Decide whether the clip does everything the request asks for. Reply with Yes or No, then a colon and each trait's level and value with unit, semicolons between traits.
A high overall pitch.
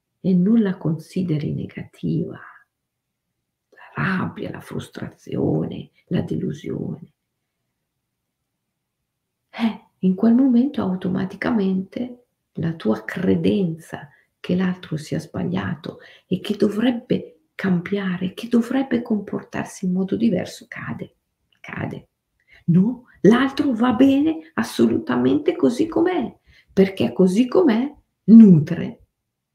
Yes: high, 205 Hz